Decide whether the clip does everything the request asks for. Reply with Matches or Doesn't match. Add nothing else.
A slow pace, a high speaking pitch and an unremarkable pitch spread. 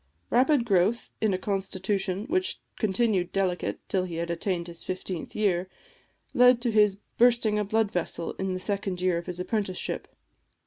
Doesn't match